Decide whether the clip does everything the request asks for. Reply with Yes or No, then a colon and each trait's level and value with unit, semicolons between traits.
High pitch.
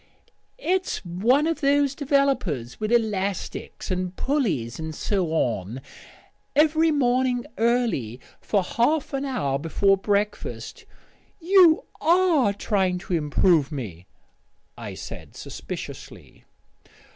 Yes: high, 215 Hz